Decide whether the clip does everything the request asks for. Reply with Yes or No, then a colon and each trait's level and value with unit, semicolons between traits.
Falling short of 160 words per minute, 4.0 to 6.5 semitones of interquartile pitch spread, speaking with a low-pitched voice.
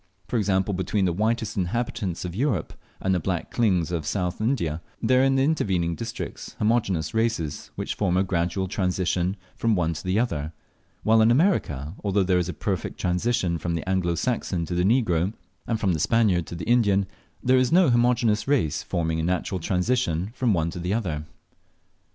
No: average, 190 wpm; average, 5.0 semitones; very low, 95 Hz